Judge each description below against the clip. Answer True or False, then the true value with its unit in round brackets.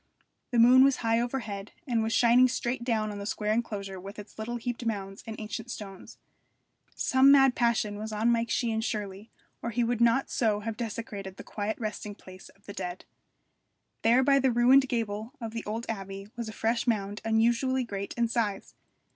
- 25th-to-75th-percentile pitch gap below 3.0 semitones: True (2.5 semitones)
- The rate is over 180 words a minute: True (190 wpm)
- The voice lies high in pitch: True (225 Hz)